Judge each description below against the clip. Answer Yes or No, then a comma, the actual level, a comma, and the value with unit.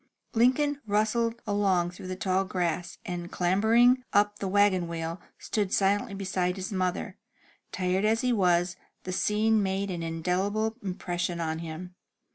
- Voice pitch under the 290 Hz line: Yes, high, 190 Hz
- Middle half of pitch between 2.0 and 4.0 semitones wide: Yes, average, 2.9 semitones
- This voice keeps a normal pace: Yes, average, 145 wpm